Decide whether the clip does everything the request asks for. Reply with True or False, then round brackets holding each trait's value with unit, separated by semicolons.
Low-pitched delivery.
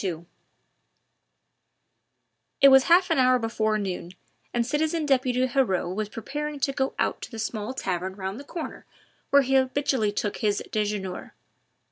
False (245 Hz)